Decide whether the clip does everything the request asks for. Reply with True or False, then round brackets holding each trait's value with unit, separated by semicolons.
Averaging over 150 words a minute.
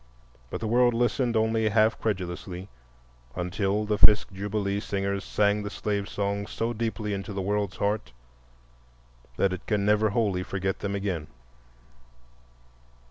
False (135 wpm)